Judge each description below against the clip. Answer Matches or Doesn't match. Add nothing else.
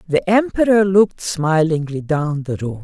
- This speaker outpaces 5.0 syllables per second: Doesn't match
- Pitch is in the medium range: Matches